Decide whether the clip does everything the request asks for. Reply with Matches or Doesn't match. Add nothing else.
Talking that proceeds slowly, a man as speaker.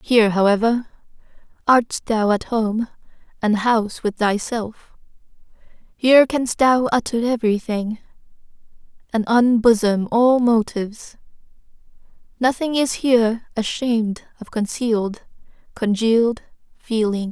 Doesn't match